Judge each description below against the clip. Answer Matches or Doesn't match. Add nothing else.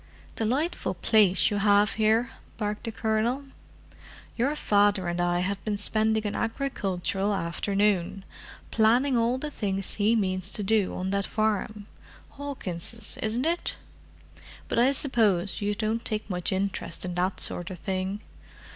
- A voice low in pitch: Doesn't match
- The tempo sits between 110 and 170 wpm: Matches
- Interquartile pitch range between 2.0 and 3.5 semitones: Matches